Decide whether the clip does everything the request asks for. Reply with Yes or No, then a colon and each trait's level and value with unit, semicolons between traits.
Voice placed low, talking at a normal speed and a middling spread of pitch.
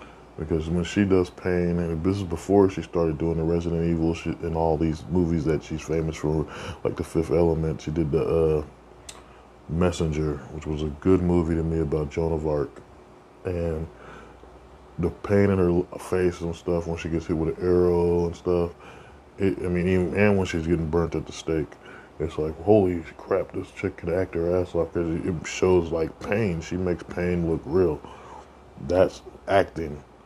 No: very low, 85 Hz; average, 190 wpm; narrow, 1.8 semitones